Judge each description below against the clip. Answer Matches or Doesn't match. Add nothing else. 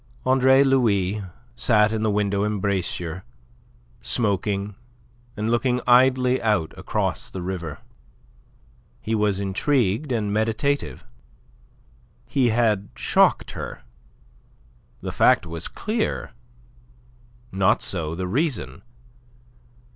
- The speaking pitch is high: Doesn't match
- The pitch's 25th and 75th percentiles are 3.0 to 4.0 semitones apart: Doesn't match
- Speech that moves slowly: Matches